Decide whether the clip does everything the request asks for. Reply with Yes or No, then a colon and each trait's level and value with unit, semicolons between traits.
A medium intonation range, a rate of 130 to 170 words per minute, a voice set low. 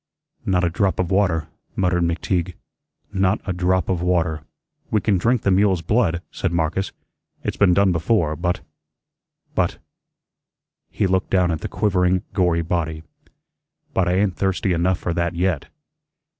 No: narrow, 2.0 semitones; average, 155 wpm; very low, 90 Hz